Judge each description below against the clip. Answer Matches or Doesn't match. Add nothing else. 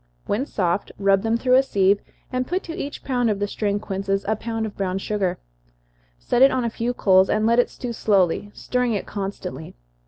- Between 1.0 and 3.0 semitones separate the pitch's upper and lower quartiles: Doesn't match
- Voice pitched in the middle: Doesn't match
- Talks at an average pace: Doesn't match